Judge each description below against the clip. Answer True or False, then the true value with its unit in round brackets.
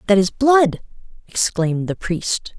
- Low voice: False (205 Hz)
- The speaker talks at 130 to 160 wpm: True (140 wpm)